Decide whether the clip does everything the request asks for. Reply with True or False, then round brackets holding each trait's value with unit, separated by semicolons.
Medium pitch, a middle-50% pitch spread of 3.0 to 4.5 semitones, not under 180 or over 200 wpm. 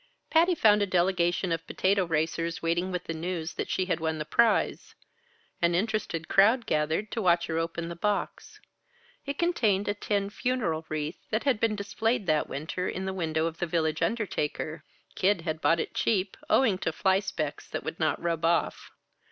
True (175 Hz; 4.0 semitones; 185 wpm)